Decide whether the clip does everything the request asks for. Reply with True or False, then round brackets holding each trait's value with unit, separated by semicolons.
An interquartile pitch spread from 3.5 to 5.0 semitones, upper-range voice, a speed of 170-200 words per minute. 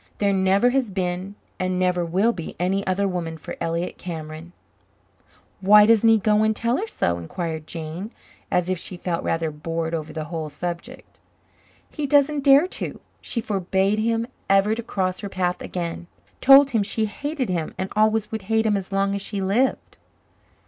True (4.1 semitones; 195 Hz; 180 wpm)